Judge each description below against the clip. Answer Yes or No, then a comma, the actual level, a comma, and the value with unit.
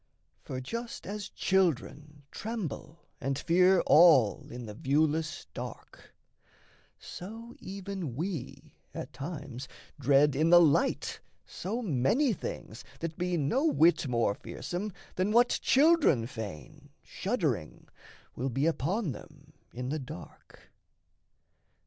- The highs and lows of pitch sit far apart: Yes, wide, 6.0 semitones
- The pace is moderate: No, slow, 115 wpm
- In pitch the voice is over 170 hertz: No, medium, 155 Hz